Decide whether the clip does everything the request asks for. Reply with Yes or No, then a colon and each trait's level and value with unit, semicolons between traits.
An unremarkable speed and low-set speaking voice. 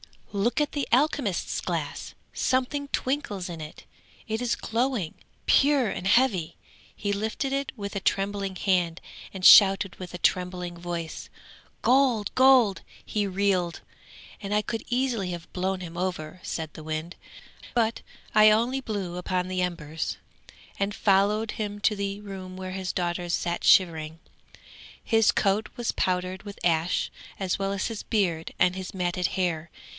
No: average, 150 wpm; high, 195 Hz